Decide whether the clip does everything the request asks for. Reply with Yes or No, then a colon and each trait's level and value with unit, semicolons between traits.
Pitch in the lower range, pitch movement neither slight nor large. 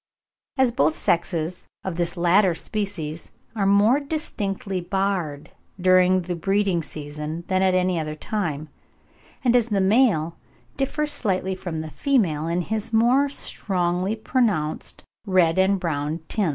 No: medium, 185 Hz; average, 4.0 semitones